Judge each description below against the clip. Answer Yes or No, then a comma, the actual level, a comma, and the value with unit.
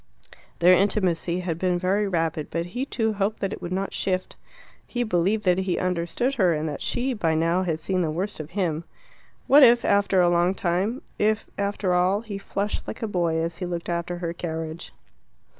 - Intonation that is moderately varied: Yes, average, 3.0 semitones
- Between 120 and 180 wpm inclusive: No, average, 200 wpm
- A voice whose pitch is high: No, medium, 180 Hz